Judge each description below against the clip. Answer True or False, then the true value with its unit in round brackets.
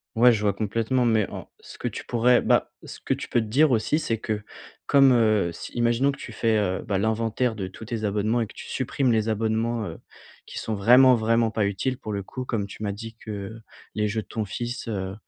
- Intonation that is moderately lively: False (2.2 semitones)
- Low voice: True (110 Hz)